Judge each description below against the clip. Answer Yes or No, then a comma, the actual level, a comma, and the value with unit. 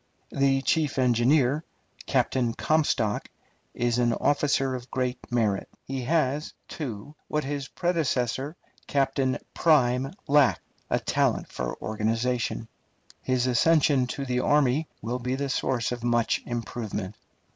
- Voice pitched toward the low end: Yes, low, 130 Hz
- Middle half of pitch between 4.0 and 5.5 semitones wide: No, average, 2.9 semitones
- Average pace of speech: No, slow, 125 wpm